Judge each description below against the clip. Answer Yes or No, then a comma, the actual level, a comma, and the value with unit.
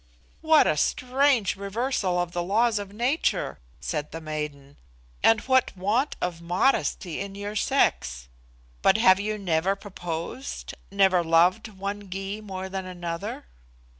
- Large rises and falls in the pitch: No, average, 3.8 semitones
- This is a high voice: Yes, high, 195 Hz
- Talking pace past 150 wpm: No, slow, 135 wpm